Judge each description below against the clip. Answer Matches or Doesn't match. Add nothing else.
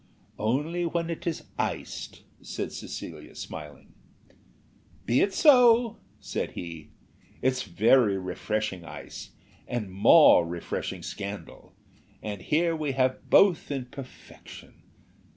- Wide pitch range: Matches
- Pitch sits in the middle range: Doesn't match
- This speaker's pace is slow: Matches